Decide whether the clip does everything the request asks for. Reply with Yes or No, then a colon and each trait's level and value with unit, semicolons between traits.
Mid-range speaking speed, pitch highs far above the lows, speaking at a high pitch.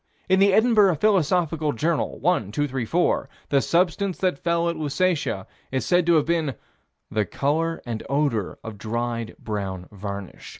No: average, 155 wpm; wide, 7.1 semitones; medium, 150 Hz